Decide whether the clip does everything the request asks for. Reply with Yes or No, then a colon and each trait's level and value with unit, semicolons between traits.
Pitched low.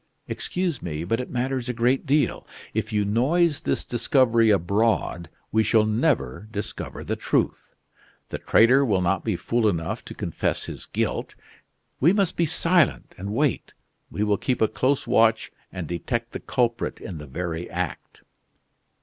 Yes: low, 115 Hz